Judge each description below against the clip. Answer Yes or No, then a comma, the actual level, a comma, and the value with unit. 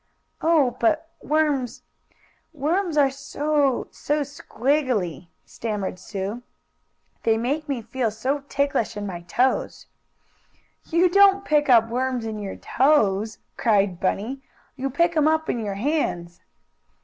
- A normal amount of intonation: No, wide, 5.8 semitones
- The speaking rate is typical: No, slow, 125 wpm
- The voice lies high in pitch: Yes, very high, 260 Hz